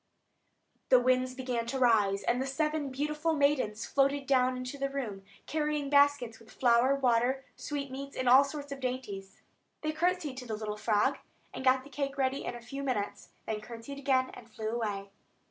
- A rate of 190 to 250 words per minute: No, average, 180 wpm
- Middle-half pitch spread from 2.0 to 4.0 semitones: Yes, average, 3.0 semitones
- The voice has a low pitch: No, very high, 260 Hz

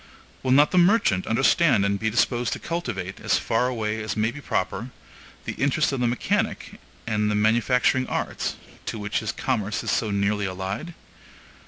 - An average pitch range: Yes, average, 4.1 semitones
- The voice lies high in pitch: No, low, 115 Hz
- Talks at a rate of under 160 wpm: No, average, 165 wpm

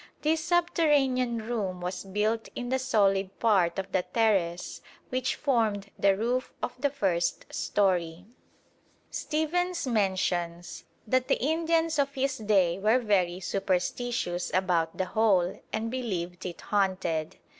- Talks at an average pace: No, slow, 130 wpm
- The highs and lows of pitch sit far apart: Yes, wide, 5.8 semitones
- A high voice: Yes, high, 210 Hz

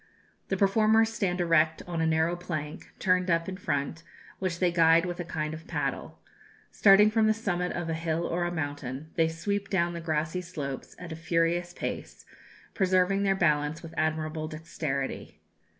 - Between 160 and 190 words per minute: Yes, average, 175 wpm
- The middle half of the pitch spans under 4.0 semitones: Yes, narrow, 2.5 semitones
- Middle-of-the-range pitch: Yes, medium, 170 Hz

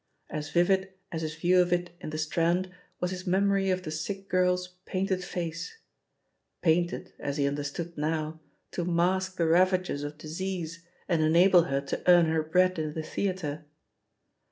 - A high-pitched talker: No, medium, 175 Hz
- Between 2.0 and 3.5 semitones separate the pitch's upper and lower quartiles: Yes, average, 2.8 semitones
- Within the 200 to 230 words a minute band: No, average, 170 wpm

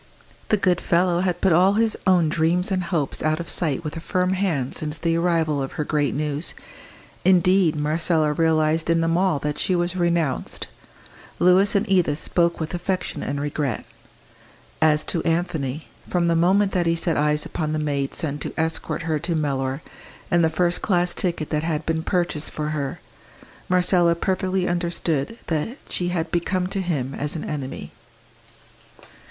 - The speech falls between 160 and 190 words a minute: Yes, average, 175 wpm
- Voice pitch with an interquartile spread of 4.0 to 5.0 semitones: No, average, 2.8 semitones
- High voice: No, medium, 165 Hz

